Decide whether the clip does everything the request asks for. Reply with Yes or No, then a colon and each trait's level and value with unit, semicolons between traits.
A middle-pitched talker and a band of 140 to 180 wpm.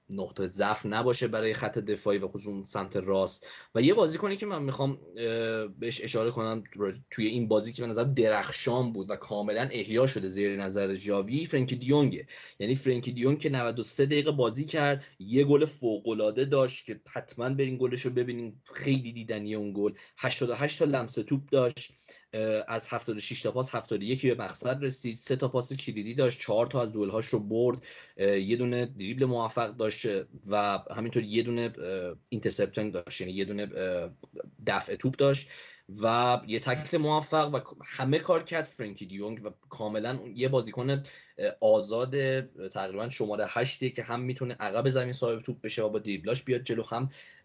No: low, 120 Hz; average, 170 wpm